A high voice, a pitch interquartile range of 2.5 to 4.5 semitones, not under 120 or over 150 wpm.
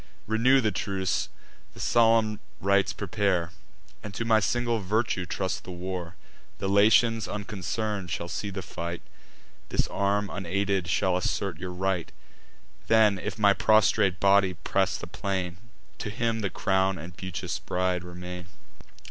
No: very low, 95 Hz; average, 2.9 semitones; average, 140 wpm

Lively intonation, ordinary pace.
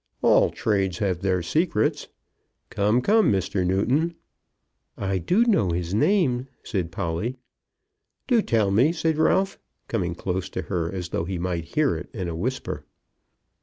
Yes: wide, 6.6 semitones; average, 145 wpm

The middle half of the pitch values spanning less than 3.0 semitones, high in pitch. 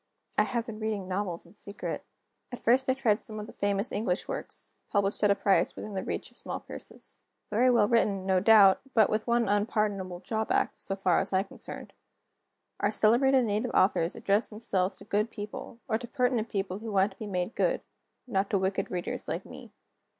Yes: narrow, 2.6 semitones; high, 205 Hz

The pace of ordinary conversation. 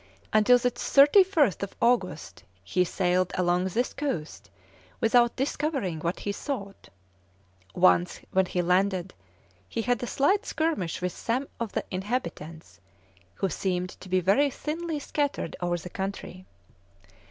No: slow, 130 wpm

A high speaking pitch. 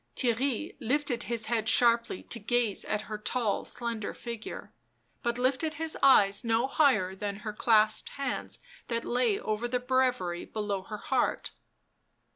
Yes: high, 235 Hz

